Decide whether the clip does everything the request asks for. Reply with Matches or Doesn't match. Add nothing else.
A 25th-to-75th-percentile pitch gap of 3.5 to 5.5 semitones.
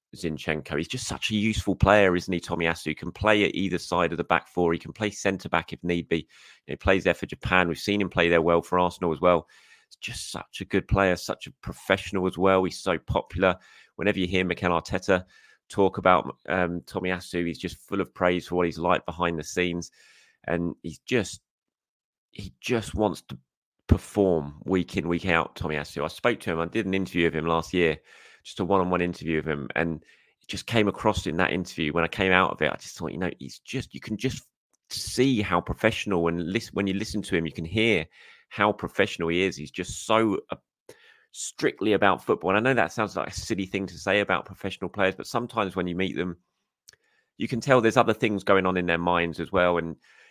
Doesn't match